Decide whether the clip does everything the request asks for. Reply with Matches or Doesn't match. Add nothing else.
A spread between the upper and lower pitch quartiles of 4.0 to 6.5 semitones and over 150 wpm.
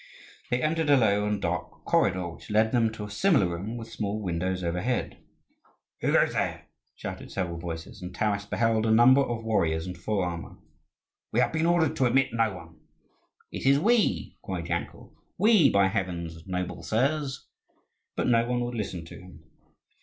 Matches